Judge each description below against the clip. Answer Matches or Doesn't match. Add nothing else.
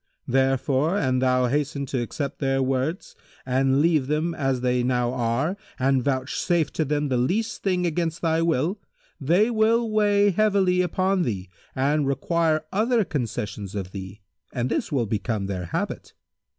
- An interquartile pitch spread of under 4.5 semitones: Doesn't match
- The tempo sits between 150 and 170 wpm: Matches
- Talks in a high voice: Doesn't match